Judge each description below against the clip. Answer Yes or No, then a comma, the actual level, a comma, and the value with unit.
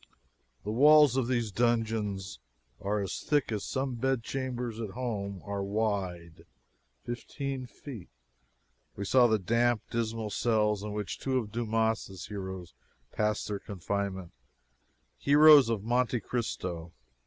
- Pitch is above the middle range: No, low, 110 Hz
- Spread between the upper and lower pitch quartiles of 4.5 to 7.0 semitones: No, average, 3.4 semitones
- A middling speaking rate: No, slow, 130 wpm